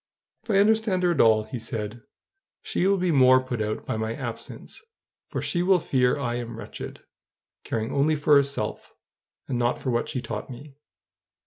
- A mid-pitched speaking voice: No, low, 130 Hz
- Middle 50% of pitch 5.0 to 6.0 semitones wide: Yes, average, 5.3 semitones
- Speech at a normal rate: Yes, average, 185 wpm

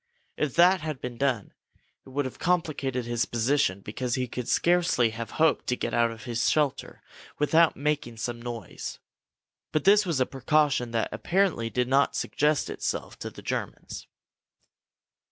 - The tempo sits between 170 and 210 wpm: No, average, 160 wpm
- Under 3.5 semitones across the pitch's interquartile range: No, average, 4.5 semitones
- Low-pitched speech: Yes, low, 130 Hz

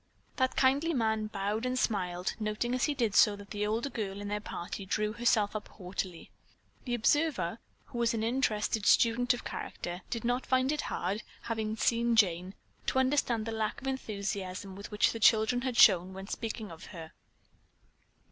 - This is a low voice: No, high, 220 Hz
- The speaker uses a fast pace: No, average, 175 wpm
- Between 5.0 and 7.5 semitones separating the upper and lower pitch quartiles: No, average, 3.2 semitones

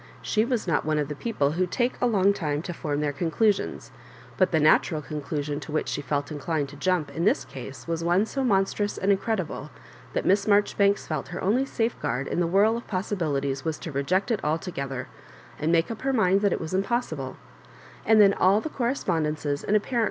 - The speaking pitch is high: No, medium, 175 Hz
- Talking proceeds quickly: Yes, fast, 210 wpm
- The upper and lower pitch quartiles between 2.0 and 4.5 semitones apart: No, wide, 5.6 semitones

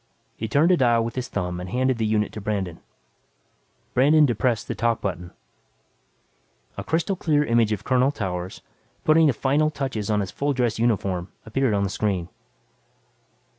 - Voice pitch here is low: Yes, low, 115 Hz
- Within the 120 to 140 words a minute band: No, average, 170 wpm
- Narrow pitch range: No, average, 5.0 semitones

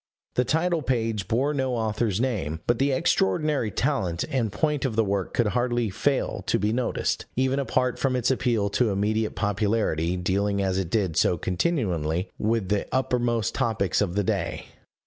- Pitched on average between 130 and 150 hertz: No, low, 110 Hz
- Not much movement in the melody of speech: No, average, 4.5 semitones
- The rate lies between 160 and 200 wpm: Yes, average, 170 wpm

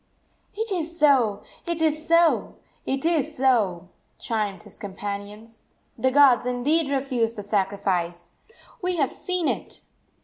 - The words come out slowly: Yes, slow, 130 wpm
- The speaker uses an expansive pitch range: Yes, wide, 7.4 semitones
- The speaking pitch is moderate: No, very high, 255 Hz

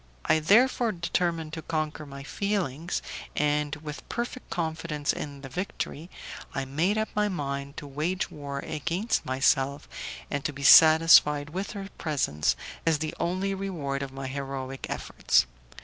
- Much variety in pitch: No, average, 4.2 semitones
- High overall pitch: No, medium, 155 Hz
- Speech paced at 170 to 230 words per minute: No, average, 150 wpm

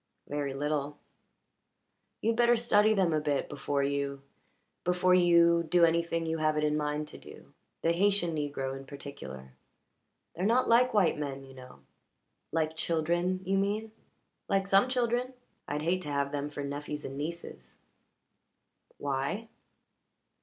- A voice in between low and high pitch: Yes, medium, 160 Hz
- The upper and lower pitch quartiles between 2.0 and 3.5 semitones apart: No, average, 5.1 semitones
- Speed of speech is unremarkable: Yes, average, 145 wpm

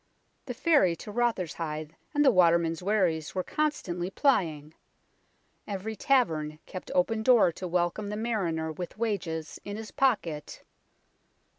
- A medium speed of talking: No, slow, 130 wpm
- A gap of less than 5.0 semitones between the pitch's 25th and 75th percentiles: No, average, 5.3 semitones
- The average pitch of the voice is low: No, medium, 185 Hz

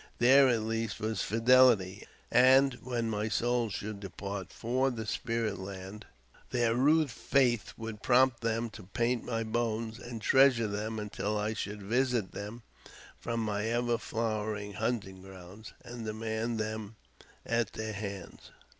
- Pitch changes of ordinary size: No, narrow, 2.3 semitones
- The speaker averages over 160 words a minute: No, average, 145 wpm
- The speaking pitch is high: No, low, 115 Hz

